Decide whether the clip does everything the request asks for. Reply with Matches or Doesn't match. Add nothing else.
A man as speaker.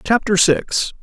Matches